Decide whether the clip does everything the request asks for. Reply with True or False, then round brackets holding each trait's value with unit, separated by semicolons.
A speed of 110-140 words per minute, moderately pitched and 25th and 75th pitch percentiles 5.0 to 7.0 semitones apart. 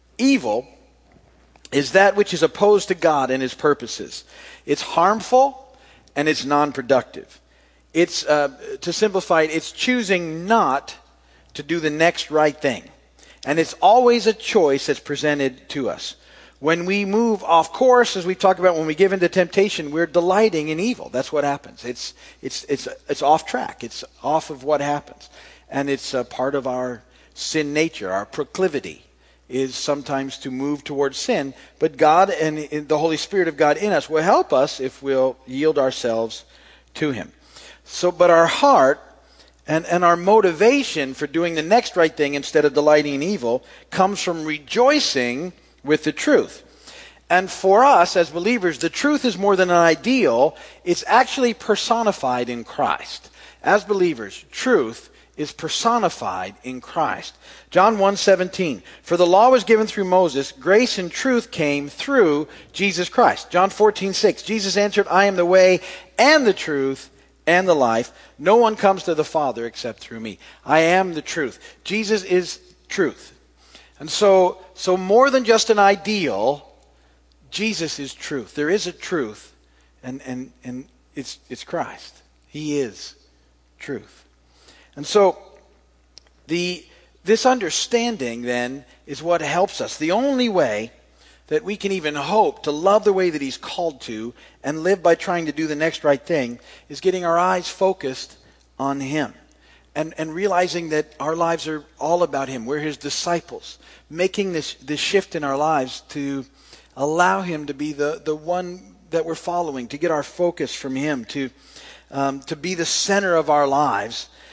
False (165 wpm; 160 Hz; 5.6 semitones)